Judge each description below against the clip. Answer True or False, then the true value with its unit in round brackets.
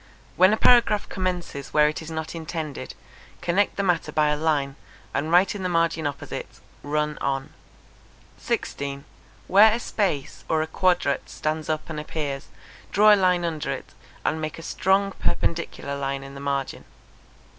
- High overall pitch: False (160 Hz)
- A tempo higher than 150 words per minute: True (165 wpm)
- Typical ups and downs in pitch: True (4.1 semitones)